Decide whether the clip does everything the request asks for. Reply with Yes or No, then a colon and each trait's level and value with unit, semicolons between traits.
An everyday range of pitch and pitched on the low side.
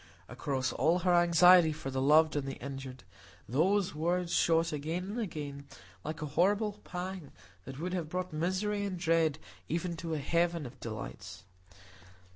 No: average, 4.0 semitones; medium, 165 Hz